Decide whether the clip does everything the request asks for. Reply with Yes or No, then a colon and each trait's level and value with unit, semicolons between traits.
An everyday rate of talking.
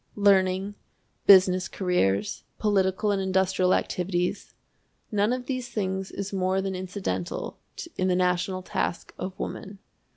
No: slow, 125 wpm